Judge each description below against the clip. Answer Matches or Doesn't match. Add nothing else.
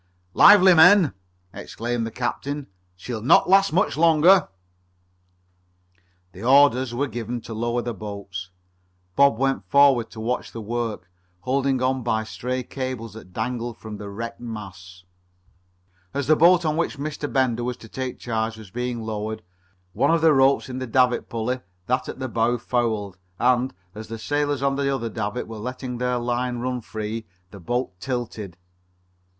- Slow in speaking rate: Doesn't match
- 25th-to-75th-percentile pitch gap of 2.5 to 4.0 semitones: Matches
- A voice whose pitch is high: Doesn't match